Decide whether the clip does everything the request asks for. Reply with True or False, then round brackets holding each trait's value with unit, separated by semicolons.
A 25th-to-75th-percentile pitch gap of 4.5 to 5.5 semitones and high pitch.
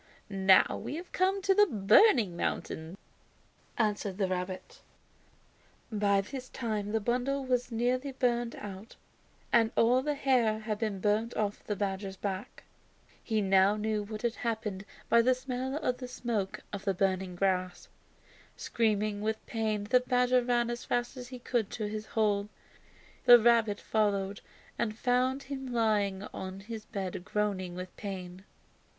False (3.7 semitones; 215 Hz)